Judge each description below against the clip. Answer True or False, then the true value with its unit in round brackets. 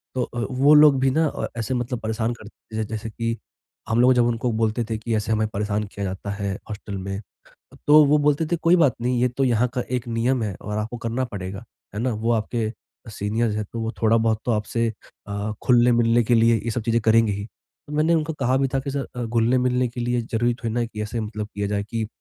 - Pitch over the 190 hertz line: False (115 Hz)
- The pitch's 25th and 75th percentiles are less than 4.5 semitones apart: True (2.5 semitones)